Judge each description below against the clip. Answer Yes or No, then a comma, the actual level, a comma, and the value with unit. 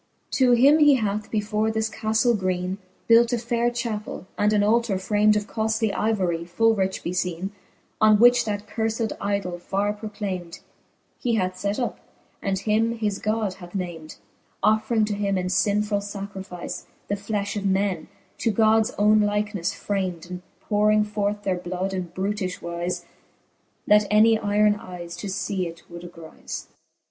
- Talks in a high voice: Yes, high, 205 Hz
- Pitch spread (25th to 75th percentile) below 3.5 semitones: Yes, average, 2.7 semitones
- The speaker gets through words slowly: No, average, 160 wpm